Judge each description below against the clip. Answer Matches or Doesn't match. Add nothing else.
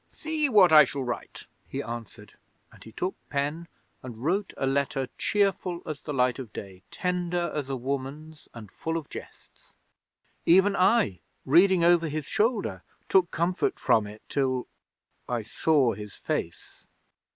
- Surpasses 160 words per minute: Doesn't match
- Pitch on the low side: Doesn't match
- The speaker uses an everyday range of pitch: Doesn't match